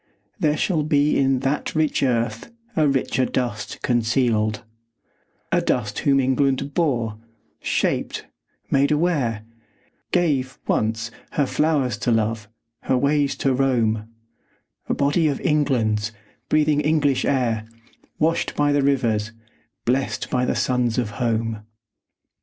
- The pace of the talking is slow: Yes, slow, 120 wpm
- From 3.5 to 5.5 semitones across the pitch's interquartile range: Yes, average, 4.1 semitones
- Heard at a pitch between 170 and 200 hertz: No, low, 130 Hz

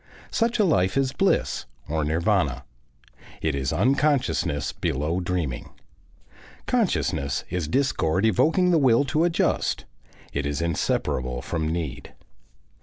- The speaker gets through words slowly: Yes, slow, 115 wpm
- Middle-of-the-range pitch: No, very low, 90 Hz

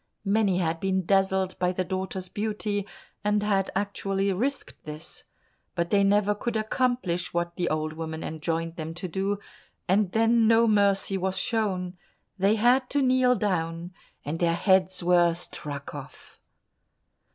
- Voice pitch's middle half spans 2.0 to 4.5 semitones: Yes, average, 3.3 semitones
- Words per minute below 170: Yes, average, 150 wpm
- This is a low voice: No, high, 190 Hz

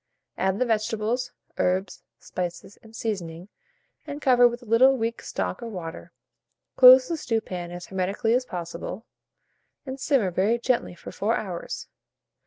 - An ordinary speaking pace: Yes, average, 145 wpm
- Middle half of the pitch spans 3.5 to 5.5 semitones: Yes, average, 5.1 semitones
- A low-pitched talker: No, high, 220 Hz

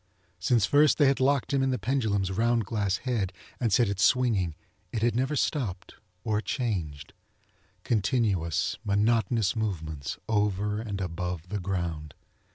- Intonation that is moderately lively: Yes, average, 4.2 semitones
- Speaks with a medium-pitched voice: No, low, 105 Hz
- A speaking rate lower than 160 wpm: Yes, average, 145 wpm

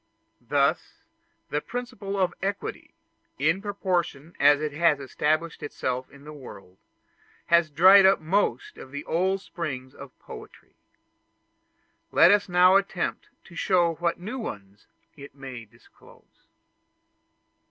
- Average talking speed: No, slow, 125 wpm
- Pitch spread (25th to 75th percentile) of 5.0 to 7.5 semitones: Yes, wide, 5.4 semitones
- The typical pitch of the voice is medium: Yes, medium, 170 Hz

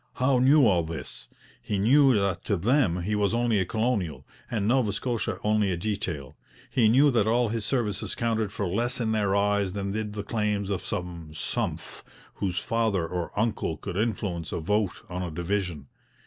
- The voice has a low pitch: Yes, low, 105 Hz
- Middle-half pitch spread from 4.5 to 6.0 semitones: No, average, 4.0 semitones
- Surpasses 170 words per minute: Yes, average, 185 wpm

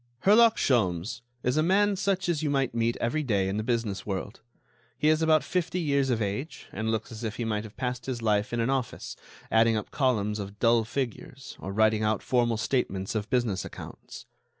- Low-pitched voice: Yes, low, 115 Hz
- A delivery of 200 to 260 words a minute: Yes, fast, 205 wpm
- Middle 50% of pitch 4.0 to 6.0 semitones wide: Yes, average, 4.3 semitones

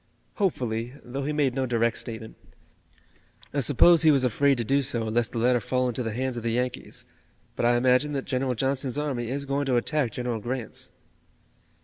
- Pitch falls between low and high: No, low, 125 Hz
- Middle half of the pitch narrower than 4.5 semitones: Yes, average, 2.7 semitones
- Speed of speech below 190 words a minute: No, average, 195 wpm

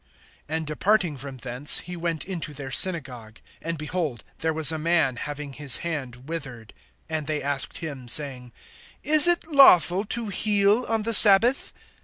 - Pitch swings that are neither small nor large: No, wide, 5.7 semitones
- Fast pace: No, average, 160 wpm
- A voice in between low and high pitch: Yes, medium, 155 Hz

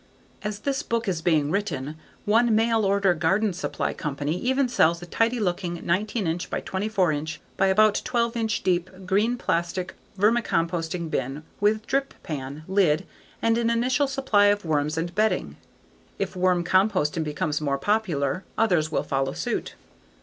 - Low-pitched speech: No, medium, 185 Hz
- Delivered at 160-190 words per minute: No, average, 150 wpm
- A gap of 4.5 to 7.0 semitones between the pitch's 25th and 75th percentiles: Yes, average, 5.3 semitones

